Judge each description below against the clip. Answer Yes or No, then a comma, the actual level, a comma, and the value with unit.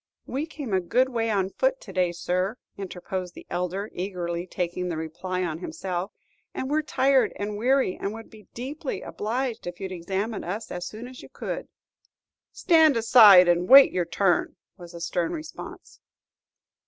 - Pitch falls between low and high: No, high, 195 Hz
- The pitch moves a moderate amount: No, wide, 5.8 semitones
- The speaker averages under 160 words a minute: No, average, 175 wpm